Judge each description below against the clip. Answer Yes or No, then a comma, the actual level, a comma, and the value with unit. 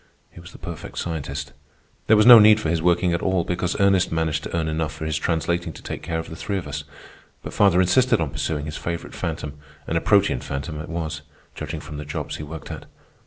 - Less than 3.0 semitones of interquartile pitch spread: Yes, narrow, 2.5 semitones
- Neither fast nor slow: No, fast, 235 wpm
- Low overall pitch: Yes, very low, 80 Hz